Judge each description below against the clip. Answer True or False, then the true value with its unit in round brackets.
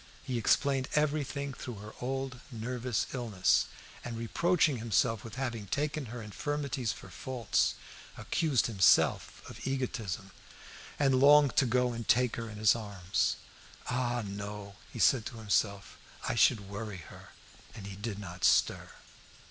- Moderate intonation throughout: True (4.1 semitones)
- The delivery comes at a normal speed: True (145 wpm)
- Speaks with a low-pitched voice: True (120 Hz)